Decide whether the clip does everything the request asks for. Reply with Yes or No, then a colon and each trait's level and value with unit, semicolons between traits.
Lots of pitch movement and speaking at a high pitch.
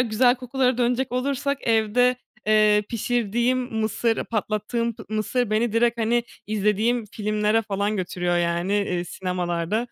No: average, 2.7 semitones; high, 220 Hz